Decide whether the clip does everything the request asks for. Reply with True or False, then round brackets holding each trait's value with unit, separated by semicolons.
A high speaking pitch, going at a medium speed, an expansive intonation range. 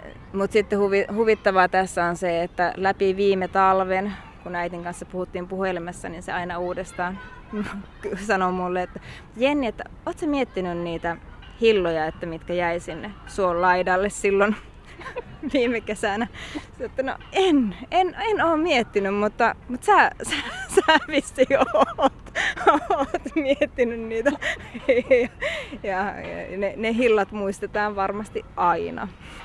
True (205 Hz; 130 wpm; 6.5 semitones)